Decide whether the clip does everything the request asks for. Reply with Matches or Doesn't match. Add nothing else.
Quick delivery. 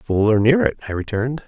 Matches